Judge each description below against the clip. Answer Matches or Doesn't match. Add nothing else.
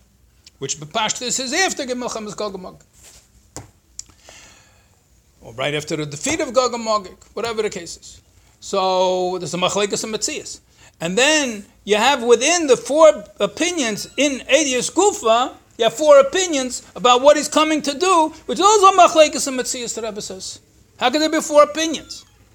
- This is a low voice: Doesn't match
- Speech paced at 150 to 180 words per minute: Matches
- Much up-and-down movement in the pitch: Matches